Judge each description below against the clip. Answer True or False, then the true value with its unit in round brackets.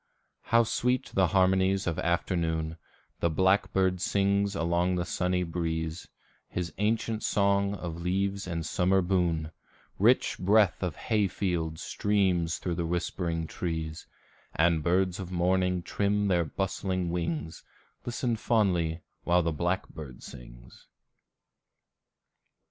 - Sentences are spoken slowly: True (120 wpm)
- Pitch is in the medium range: False (90 Hz)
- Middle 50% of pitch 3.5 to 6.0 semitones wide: False (2.7 semitones)